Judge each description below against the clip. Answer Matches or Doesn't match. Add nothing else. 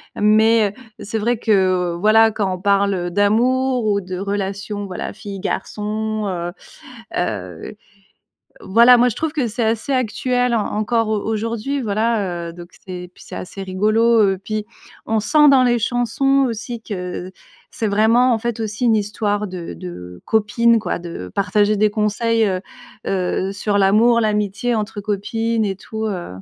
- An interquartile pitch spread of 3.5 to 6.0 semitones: Doesn't match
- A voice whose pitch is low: Doesn't match